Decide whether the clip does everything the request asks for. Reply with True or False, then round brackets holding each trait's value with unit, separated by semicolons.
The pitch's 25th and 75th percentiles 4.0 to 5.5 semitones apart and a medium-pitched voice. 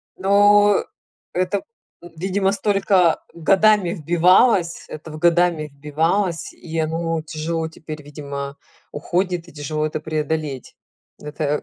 False (3.1 semitones; 165 Hz)